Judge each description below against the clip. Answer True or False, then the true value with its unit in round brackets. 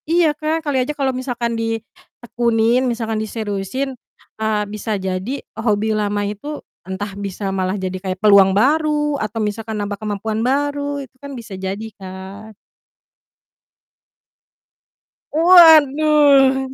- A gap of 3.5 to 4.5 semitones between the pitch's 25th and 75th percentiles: False (5.3 semitones)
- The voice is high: True (225 Hz)